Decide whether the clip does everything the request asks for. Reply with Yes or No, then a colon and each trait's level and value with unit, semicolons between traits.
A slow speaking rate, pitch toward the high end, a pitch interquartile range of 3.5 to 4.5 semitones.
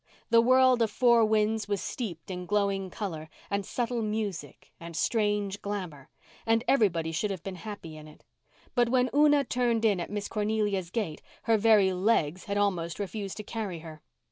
No: average, 175 wpm; high, 205 Hz; average, 3.8 semitones